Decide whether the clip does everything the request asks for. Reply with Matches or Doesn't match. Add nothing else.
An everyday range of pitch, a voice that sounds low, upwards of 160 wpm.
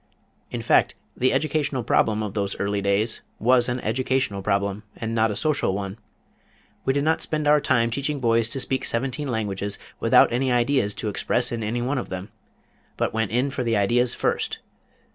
Matches